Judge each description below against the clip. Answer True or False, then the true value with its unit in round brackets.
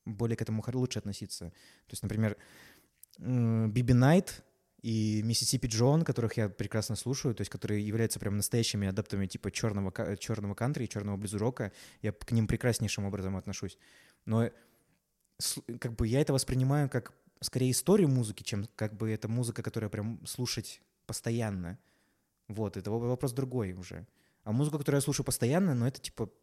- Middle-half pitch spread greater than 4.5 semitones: False (3.1 semitones)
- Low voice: True (115 Hz)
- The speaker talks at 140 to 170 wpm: True (160 wpm)